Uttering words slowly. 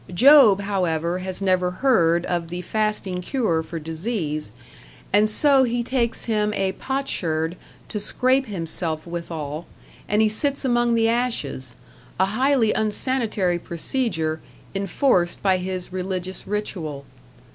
Yes: slow, 125 wpm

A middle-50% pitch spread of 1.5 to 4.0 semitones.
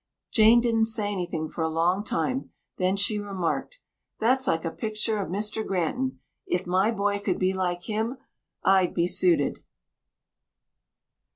Yes: average, 3.7 semitones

